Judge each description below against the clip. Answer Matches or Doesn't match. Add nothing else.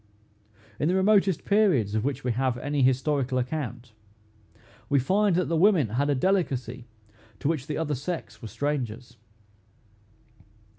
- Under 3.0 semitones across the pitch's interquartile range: Doesn't match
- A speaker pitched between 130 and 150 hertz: Matches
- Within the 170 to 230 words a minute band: Doesn't match